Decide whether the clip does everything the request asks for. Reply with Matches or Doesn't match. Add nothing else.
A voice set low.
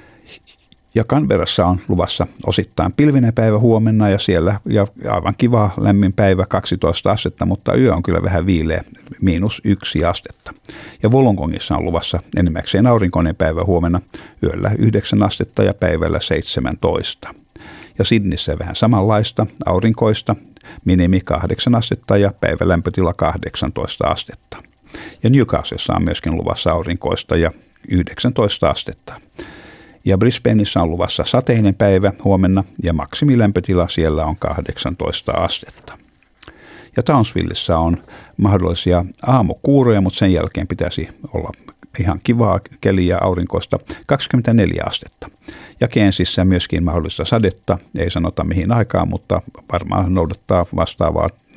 Matches